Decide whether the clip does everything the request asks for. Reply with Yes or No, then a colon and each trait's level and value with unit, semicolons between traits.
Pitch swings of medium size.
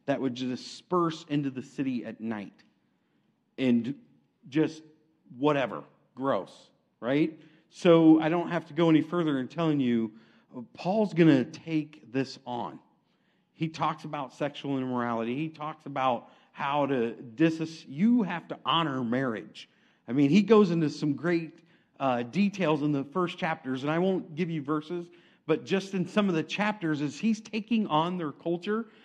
Yes: average, 3.6 semitones